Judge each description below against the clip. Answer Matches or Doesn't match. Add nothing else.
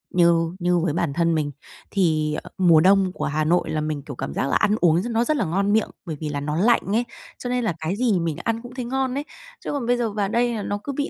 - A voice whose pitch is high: Doesn't match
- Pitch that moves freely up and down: Matches